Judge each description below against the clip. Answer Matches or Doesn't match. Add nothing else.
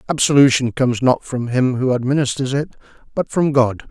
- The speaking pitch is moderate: Doesn't match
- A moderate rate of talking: Matches